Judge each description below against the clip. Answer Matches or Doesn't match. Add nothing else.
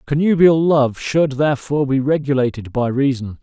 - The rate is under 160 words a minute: Matches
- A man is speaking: Matches